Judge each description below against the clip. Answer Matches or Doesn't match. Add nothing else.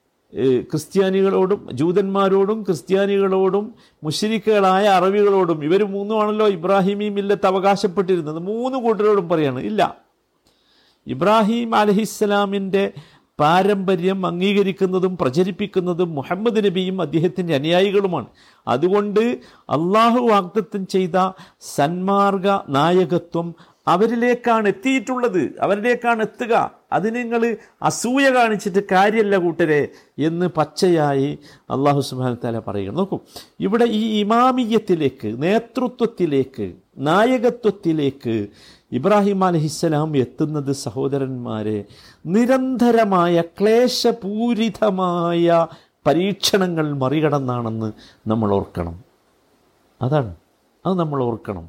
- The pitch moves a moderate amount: Doesn't match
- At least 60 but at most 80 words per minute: Matches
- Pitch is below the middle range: Doesn't match